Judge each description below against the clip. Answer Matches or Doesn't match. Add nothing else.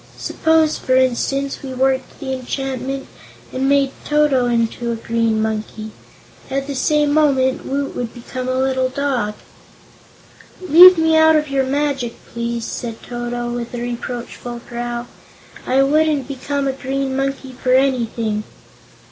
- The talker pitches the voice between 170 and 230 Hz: Doesn't match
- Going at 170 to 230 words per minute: Doesn't match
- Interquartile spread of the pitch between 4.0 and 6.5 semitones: Doesn't match